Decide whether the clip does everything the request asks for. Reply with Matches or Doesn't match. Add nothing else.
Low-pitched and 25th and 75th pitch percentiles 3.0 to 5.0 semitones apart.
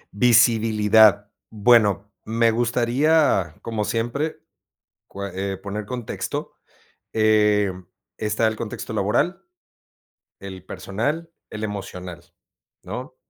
Doesn't match